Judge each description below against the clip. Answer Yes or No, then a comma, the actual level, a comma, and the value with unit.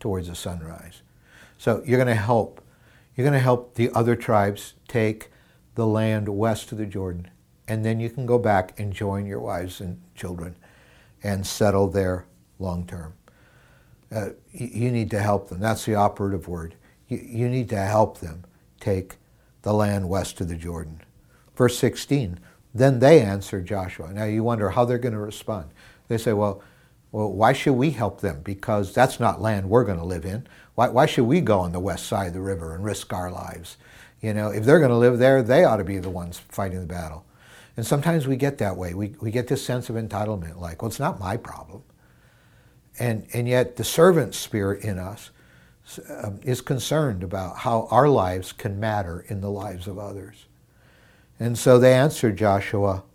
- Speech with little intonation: No, average, 4.2 semitones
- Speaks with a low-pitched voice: Yes, low, 105 Hz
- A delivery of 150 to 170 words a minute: No, average, 195 wpm